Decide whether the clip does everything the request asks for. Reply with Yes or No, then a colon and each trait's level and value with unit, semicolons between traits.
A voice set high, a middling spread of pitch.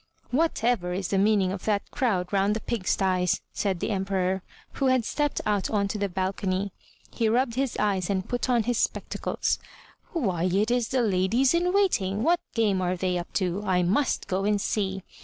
Yes: high, 200 Hz; average, 4.1 semitones